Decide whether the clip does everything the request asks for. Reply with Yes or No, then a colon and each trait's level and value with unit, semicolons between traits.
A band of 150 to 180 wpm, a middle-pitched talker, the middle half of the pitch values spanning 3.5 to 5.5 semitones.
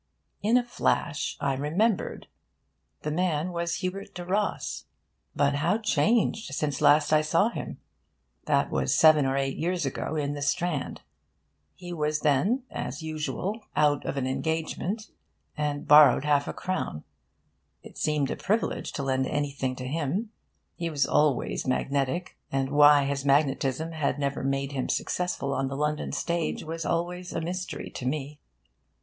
Yes: average, 155 wpm; medium, 150 Hz; average, 4.0 semitones